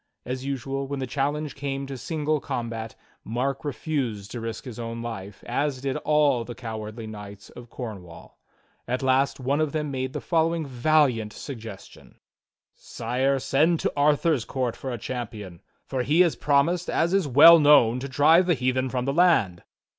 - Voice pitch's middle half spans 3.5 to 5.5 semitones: Yes, average, 4.1 semitones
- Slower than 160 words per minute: No, average, 175 wpm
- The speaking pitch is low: Yes, low, 130 Hz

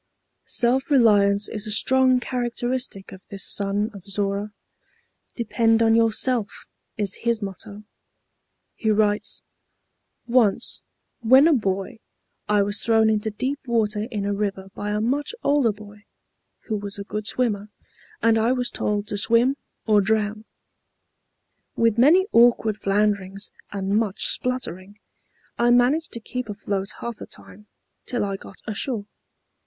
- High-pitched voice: Yes, high, 215 Hz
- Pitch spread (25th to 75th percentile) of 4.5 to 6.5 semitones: No, average, 2.8 semitones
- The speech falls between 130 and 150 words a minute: Yes, average, 140 wpm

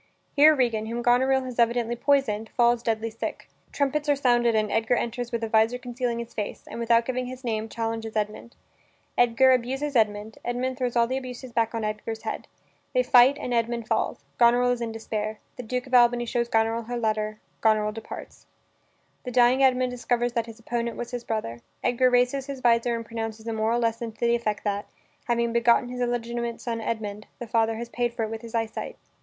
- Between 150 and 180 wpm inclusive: No, average, 200 wpm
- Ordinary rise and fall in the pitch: No, narrow, 1.7 semitones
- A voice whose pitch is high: Yes, high, 235 Hz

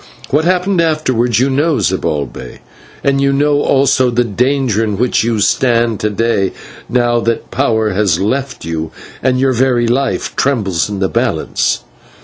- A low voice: Yes, low, 120 Hz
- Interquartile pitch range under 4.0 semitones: No, average, 4.3 semitones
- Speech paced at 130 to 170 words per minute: Yes, average, 155 wpm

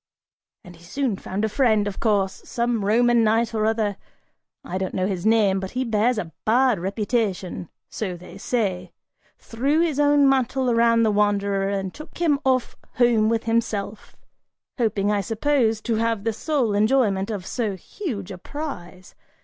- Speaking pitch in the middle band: No, high, 220 Hz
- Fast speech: No, average, 165 wpm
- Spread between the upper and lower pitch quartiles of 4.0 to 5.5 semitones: No, average, 3.4 semitones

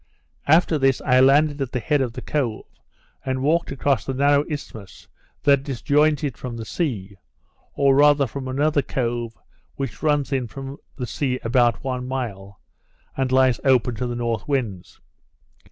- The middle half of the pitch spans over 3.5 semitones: No, average, 2.9 semitones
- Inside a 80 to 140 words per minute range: No, average, 165 wpm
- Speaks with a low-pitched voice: Yes, low, 130 Hz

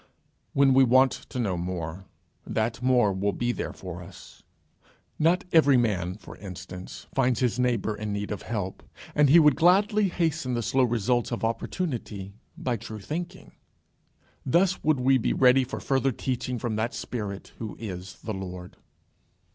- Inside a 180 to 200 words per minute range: No, average, 165 wpm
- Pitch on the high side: No, low, 120 Hz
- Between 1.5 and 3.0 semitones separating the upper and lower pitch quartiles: No, average, 4.9 semitones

